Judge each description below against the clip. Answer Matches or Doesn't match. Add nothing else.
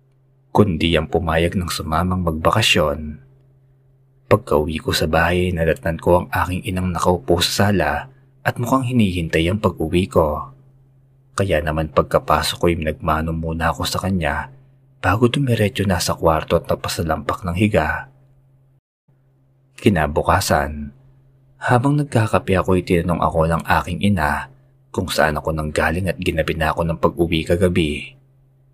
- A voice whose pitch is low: Matches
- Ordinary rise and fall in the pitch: Doesn't match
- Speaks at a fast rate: Doesn't match